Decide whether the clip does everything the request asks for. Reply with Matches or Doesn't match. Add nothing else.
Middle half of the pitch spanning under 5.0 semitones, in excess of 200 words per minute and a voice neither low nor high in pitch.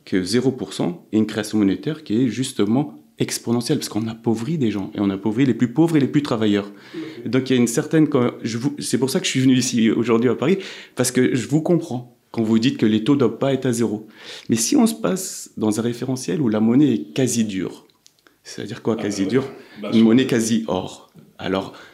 Doesn't match